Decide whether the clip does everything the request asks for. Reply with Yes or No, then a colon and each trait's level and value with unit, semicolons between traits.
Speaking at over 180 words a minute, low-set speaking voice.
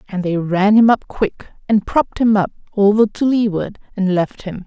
No: fast, 205 wpm; high, 205 Hz